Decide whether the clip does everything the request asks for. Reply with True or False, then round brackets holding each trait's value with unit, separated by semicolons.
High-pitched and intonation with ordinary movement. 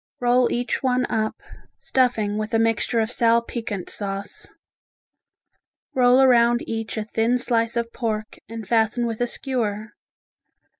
False (230 Hz; 2.0 semitones)